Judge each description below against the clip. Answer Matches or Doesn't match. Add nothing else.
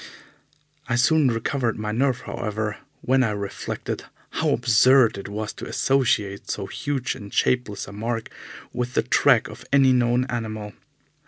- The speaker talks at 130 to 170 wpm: Matches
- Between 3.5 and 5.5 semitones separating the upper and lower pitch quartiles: Doesn't match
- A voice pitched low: Matches